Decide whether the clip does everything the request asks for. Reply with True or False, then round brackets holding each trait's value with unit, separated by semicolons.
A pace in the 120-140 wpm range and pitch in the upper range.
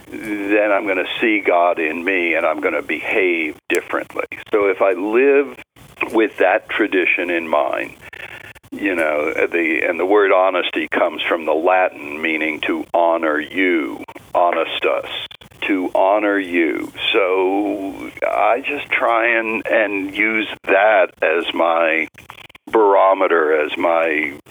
True (135 wpm; 315 Hz)